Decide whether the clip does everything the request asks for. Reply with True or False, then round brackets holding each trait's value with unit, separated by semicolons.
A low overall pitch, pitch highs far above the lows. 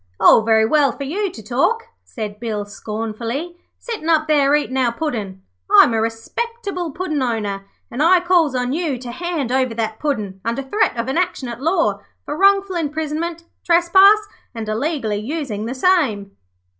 False (275 Hz; 7.1 semitones)